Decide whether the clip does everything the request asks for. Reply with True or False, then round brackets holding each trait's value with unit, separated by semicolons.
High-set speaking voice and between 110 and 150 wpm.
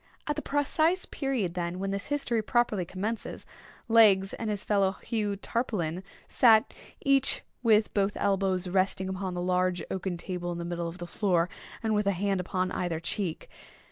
False (195 Hz; 170 wpm)